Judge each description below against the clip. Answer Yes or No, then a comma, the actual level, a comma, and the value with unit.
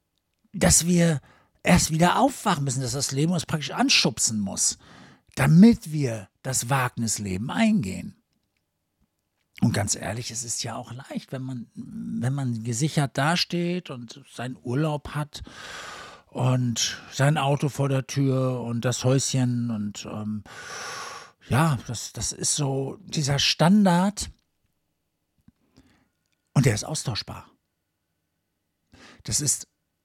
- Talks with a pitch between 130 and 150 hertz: Yes, low, 135 Hz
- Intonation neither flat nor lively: No, wide, 5.9 semitones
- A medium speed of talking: No, slow, 120 wpm